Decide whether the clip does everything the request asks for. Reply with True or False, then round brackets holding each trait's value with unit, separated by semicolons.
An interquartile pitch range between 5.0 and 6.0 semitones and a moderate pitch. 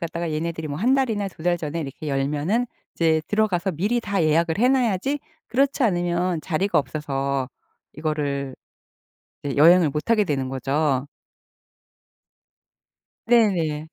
True (5.4 semitones; 165 Hz)